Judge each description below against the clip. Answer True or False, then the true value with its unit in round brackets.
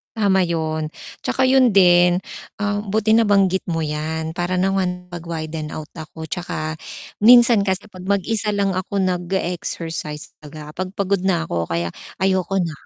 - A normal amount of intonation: True (3.6 semitones)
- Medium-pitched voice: True (180 Hz)